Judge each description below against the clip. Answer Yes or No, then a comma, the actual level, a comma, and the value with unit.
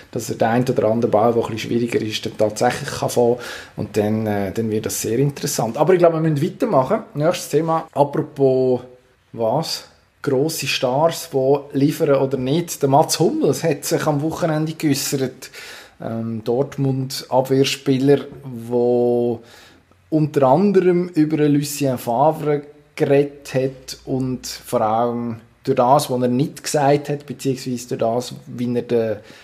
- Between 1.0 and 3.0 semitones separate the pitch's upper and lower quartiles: No, average, 3.6 semitones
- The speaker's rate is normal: Yes, average, 150 wpm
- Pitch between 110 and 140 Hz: Yes, low, 135 Hz